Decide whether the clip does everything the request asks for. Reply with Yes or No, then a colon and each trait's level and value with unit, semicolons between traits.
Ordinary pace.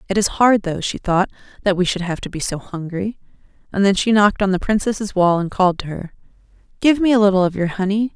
No: fast, 245 wpm